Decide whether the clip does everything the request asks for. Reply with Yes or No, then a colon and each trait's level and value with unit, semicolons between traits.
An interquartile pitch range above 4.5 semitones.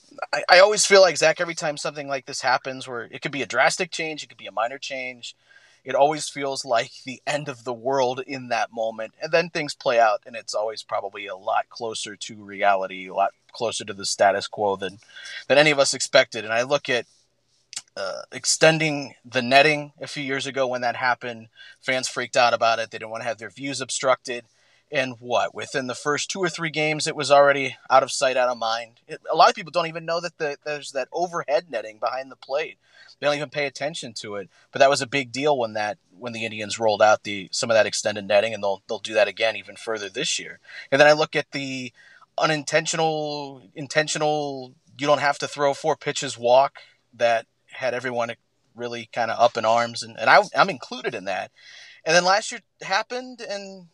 No: average, 4.2 semitones